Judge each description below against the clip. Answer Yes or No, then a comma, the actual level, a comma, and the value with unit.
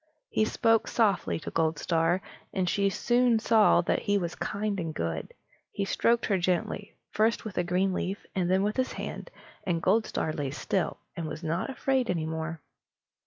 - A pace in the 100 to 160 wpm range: No, average, 170 wpm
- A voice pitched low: No, high, 190 Hz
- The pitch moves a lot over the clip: No, average, 4.5 semitones